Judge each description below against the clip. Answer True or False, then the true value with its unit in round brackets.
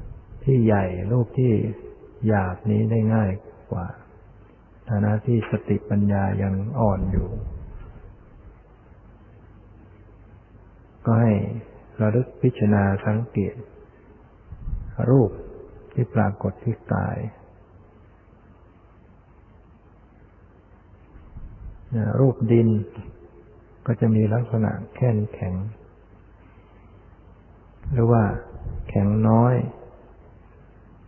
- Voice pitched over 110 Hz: False (105 Hz)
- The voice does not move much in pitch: True (2.3 semitones)